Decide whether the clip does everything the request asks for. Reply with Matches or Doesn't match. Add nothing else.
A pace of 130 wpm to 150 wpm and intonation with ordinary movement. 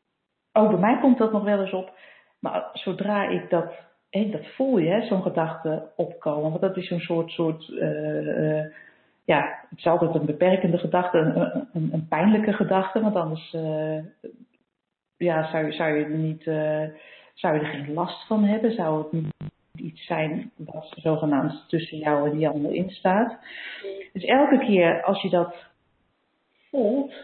Doesn't match